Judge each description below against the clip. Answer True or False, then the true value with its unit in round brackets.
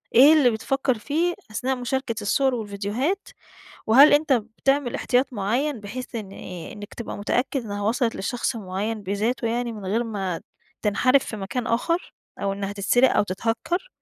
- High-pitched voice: True (230 Hz)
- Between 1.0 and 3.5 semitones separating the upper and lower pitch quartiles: False (4.4 semitones)